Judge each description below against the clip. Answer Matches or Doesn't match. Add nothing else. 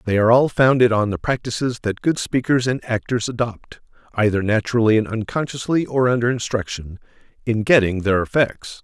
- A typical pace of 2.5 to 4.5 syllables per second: Doesn't match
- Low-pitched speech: Matches